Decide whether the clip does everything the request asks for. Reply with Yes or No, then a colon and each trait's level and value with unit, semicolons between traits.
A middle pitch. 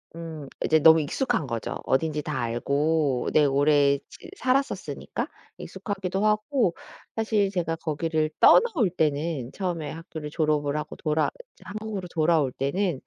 Yes: medium, 160 Hz